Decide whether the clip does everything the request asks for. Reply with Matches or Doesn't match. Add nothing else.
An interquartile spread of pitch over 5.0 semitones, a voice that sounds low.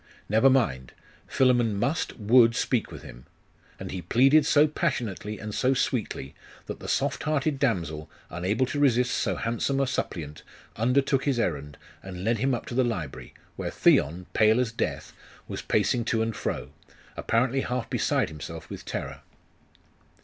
Matches